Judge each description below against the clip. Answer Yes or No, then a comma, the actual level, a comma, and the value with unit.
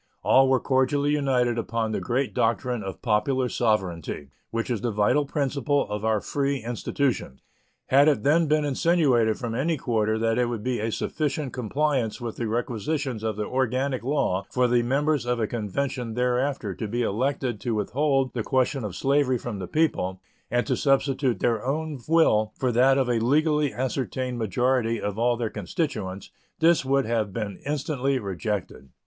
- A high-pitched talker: No, low, 125 Hz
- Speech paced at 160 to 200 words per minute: Yes, average, 175 wpm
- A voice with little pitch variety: No, average, 3.8 semitones